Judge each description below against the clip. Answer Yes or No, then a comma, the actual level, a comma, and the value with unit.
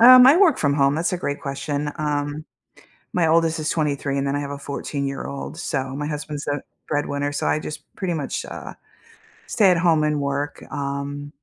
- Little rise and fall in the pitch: Yes, narrow, 2.0 semitones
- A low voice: No, medium, 145 Hz